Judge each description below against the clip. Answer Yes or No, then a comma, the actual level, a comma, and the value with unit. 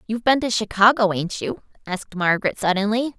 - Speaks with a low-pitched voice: No, high, 215 Hz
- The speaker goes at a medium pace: Yes, average, 170 wpm